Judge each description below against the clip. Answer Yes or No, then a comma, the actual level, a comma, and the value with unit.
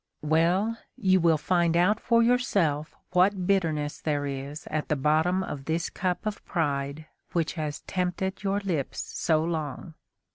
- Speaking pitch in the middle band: Yes, medium, 170 Hz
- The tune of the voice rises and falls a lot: No, average, 3.8 semitones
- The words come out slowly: No, average, 150 wpm